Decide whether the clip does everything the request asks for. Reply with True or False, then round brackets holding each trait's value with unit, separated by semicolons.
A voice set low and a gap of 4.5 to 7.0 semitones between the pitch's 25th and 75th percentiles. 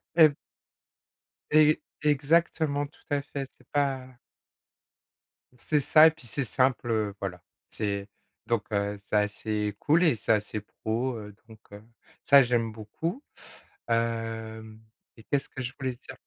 True (120 Hz; 4.9 semitones)